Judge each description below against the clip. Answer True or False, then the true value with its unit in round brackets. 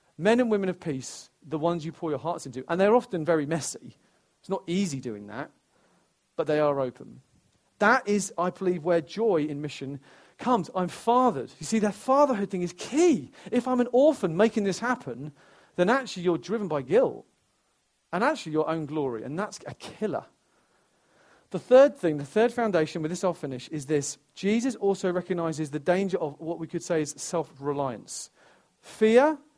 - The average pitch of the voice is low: False (175 Hz)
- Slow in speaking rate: False (185 wpm)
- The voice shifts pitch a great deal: True (6.0 semitones)